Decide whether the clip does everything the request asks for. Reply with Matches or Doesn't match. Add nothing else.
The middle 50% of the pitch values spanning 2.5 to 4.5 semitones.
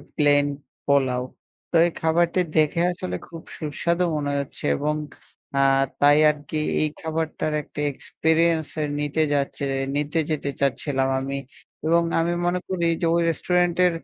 Matches